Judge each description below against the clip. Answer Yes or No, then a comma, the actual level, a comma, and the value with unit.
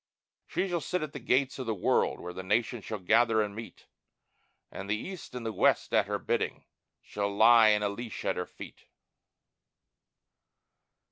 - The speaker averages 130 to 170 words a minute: No, average, 180 wpm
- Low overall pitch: Yes, low, 115 Hz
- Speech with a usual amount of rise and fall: Yes, average, 3.4 semitones